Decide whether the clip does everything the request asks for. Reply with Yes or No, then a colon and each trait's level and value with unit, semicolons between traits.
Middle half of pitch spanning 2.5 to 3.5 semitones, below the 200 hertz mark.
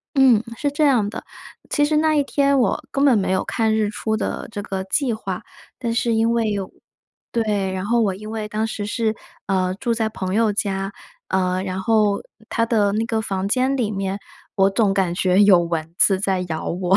No: average, 3.2 semitones; high, 210 Hz